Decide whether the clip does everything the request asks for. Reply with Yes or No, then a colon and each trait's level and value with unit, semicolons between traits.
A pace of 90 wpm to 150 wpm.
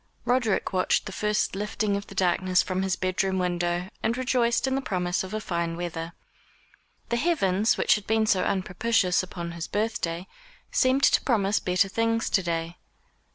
No: average, 175 wpm